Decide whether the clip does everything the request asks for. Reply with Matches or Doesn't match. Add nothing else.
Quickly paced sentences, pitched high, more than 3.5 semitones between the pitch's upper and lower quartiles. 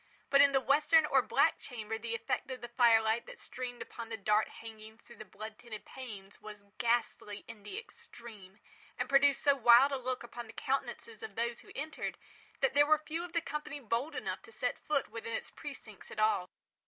Matches